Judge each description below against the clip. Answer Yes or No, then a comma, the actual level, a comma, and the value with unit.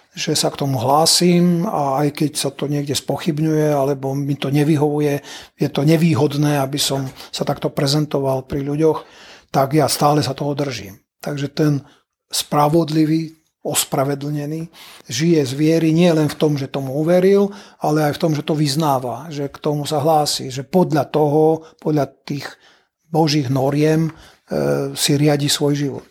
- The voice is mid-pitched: Yes, medium, 150 Hz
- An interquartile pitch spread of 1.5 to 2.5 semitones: Yes, narrow, 2.0 semitones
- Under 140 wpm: No, average, 160 wpm